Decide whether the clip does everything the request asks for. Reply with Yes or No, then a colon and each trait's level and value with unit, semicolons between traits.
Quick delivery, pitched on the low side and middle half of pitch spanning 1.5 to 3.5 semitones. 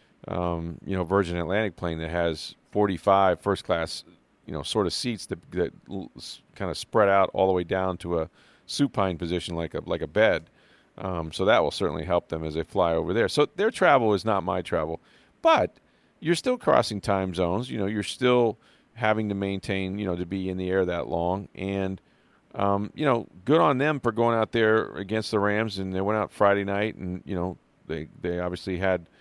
Yes: fast, 210 wpm; very low, 95 Hz; average, 3.1 semitones